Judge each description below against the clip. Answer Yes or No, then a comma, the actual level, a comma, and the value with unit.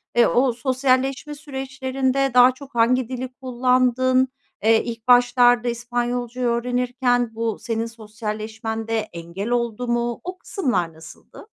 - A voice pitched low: No, high, 245 Hz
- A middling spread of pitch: No, narrow, 2.0 semitones